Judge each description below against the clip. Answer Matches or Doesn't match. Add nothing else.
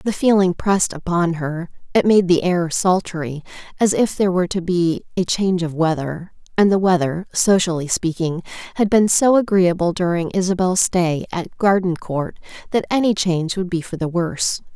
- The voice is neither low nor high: Matches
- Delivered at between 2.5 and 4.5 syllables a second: Doesn't match